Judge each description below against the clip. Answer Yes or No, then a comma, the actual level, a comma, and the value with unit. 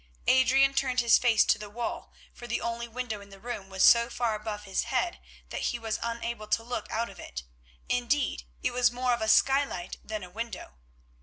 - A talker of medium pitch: No, high, 235 Hz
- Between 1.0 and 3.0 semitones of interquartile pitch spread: Yes, narrow, 2.5 semitones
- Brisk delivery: Yes, fast, 210 wpm